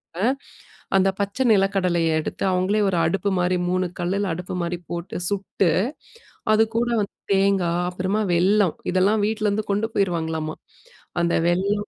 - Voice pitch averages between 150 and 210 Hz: Yes, high, 190 Hz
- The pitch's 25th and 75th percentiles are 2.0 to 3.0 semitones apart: Yes, narrow, 2.4 semitones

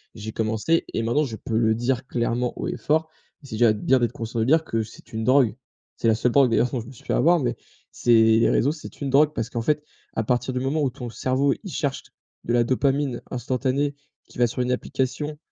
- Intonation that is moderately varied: Yes, average, 3.4 semitones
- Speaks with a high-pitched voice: No, low, 125 Hz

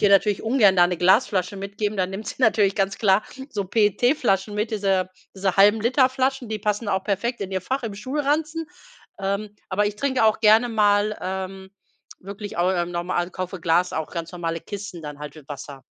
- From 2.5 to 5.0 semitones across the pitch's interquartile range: Yes, average, 2.9 semitones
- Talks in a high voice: Yes, high, 200 Hz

